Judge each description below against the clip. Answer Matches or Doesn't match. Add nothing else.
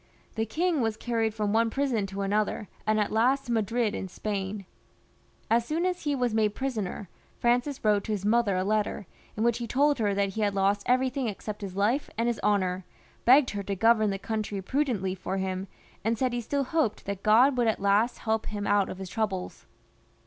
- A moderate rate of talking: Doesn't match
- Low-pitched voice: Doesn't match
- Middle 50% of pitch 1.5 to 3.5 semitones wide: Matches